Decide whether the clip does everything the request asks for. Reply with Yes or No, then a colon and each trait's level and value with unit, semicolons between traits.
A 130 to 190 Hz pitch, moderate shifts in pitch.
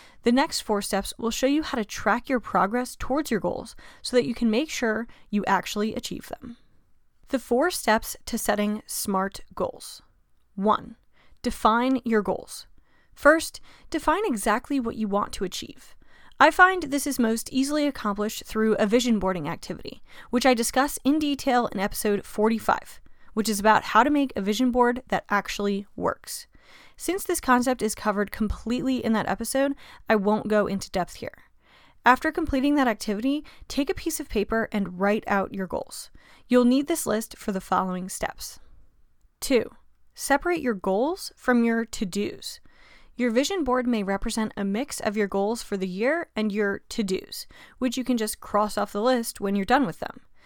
No: high, 230 Hz; average, 4.1 semitones